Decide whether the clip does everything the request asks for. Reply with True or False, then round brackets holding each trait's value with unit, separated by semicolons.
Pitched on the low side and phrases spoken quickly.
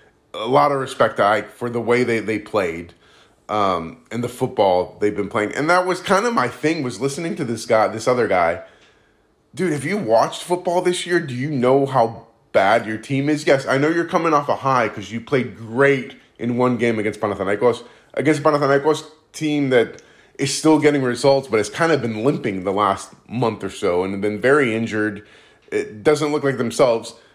True (125 Hz; 210 wpm)